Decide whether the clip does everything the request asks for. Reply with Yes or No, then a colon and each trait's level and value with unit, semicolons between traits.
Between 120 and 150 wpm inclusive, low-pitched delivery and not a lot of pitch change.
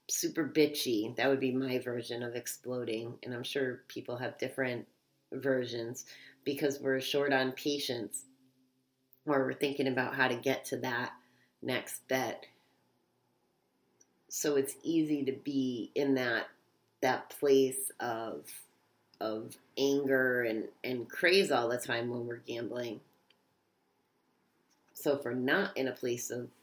Yes: slow, 135 wpm; low, 130 Hz; narrow, 2.2 semitones